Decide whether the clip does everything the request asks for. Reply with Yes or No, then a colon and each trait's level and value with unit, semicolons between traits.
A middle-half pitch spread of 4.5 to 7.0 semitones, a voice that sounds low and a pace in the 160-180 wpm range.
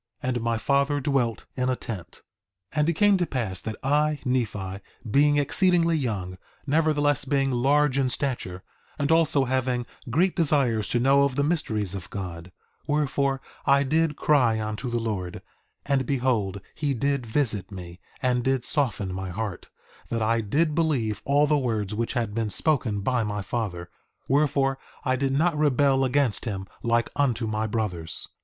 Yes: average, 4.8 semitones; low, 130 Hz; average, 170 wpm